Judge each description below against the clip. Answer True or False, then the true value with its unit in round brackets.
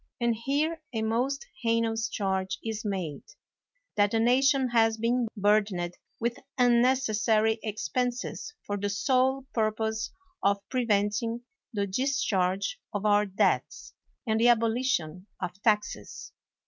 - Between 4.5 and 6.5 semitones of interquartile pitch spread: False (3.1 semitones)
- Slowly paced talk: True (125 wpm)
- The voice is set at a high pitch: True (225 Hz)